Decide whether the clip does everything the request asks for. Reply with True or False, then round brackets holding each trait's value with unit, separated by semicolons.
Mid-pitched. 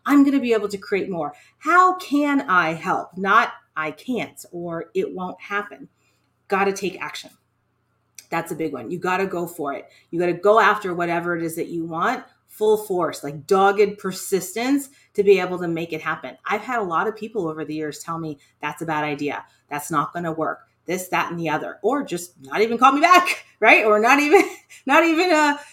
True (180 Hz)